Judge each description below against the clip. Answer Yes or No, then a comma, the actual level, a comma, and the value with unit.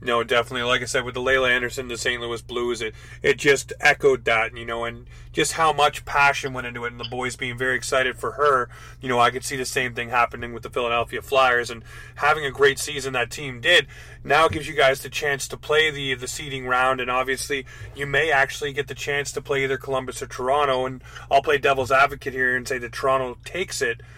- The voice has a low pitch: Yes, low, 130 Hz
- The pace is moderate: No, fast, 240 wpm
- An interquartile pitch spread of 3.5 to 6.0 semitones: No, narrow, 2.5 semitones